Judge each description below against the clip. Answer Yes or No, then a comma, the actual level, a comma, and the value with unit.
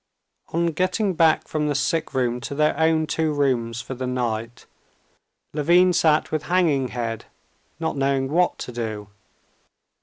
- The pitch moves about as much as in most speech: Yes, average, 4.6 semitones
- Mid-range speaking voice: Yes, medium, 145 Hz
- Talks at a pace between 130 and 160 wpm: Yes, average, 150 wpm